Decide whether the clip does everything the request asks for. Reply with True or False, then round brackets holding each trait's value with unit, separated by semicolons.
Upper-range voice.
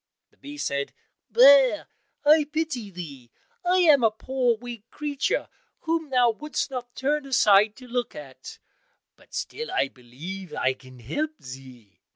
True (245 Hz)